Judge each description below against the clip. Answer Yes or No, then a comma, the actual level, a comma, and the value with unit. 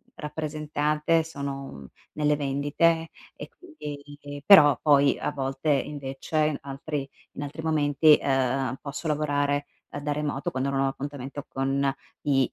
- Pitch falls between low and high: Yes, medium, 145 Hz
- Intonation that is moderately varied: No, narrow, 1.7 semitones